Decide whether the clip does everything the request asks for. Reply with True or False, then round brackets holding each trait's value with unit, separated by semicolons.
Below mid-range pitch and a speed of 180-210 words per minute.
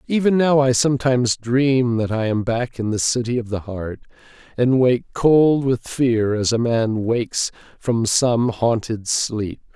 False (120 Hz; 170 wpm)